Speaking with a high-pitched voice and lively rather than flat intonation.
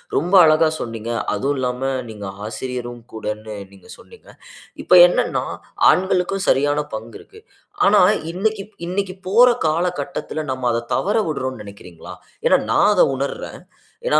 No: medium, 140 Hz; wide, 8.1 semitones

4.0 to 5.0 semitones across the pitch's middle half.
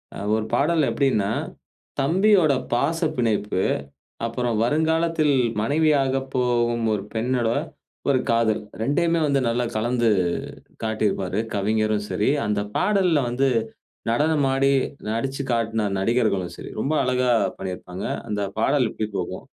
Yes: average, 4.6 semitones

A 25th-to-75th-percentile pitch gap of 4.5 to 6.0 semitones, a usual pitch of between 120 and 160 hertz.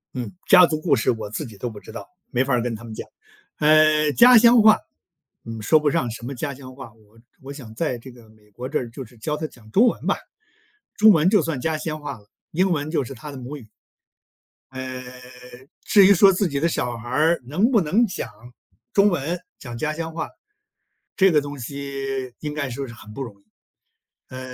Yes: average, 5.0 semitones; medium, 140 Hz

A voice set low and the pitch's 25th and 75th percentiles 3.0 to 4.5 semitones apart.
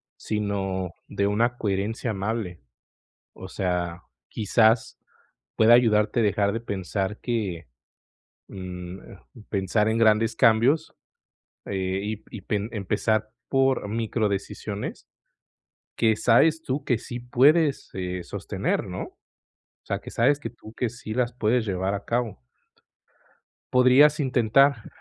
Yes: low, 110 Hz; average, 3.5 semitones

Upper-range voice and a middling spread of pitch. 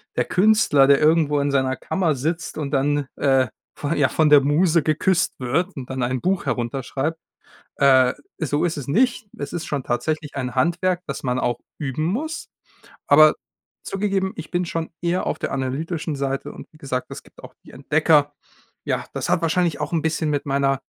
No: medium, 150 Hz; average, 3.6 semitones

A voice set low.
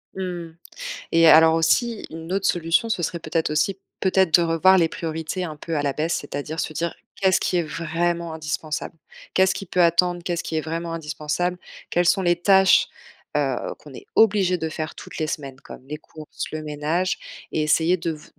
No: medium, 165 Hz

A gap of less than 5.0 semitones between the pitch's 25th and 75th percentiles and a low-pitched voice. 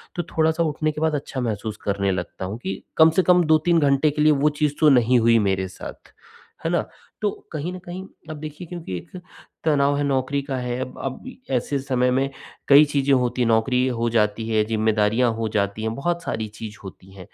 No: wide, 5.4 semitones; low, 130 Hz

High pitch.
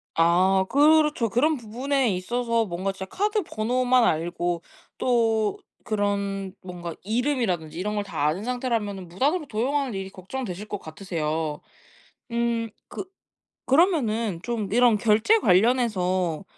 Yes: high, 215 Hz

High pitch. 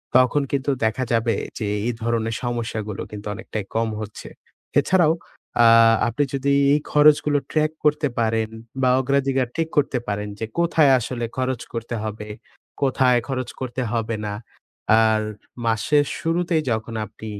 No: low, 120 Hz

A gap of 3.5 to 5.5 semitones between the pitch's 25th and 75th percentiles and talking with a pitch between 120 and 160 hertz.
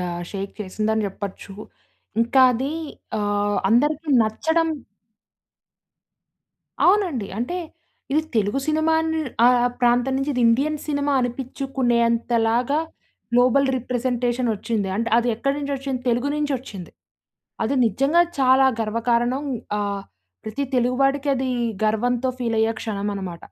No: average, 3.8 semitones; high, 245 Hz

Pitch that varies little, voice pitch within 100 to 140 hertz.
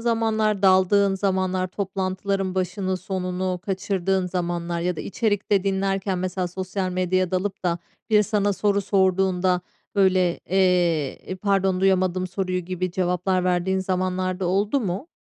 No: narrow, 1.2 semitones; medium, 185 Hz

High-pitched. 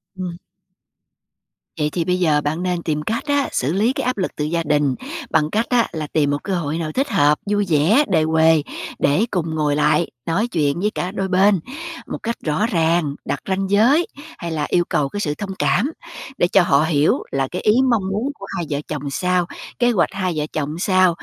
No: medium, 170 Hz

